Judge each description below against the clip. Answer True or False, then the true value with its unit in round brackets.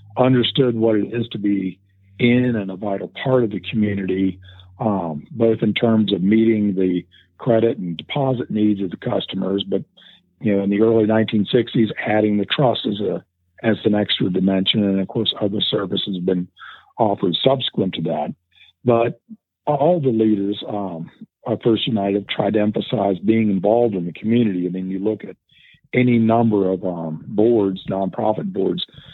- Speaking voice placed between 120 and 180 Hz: False (105 Hz)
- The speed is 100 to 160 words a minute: False (170 wpm)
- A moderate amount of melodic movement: True (3.0 semitones)